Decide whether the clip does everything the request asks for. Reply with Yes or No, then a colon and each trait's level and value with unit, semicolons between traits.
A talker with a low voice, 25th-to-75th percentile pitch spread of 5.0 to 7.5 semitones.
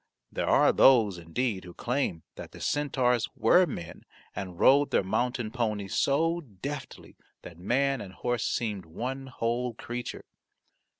Yes: low, 120 Hz; average, 5.3 semitones